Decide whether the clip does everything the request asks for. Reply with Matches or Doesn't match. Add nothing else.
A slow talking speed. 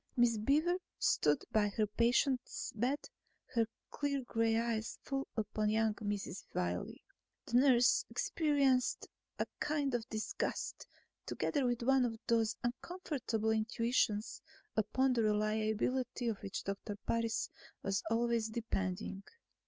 Matches